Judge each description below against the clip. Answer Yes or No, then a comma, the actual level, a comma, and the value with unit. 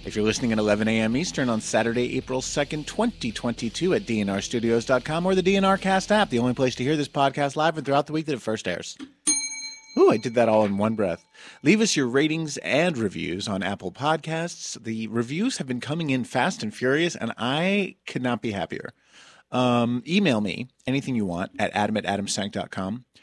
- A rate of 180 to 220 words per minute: Yes, average, 200 wpm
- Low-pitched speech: Yes, low, 130 Hz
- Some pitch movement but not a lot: No, wide, 5.9 semitones